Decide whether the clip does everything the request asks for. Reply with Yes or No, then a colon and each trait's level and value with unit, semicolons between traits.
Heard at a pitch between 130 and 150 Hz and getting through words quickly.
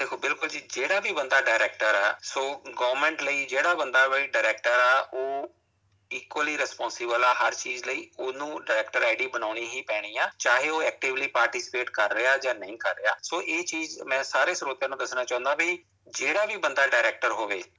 Yes: medium, 140 Hz; fast, 185 wpm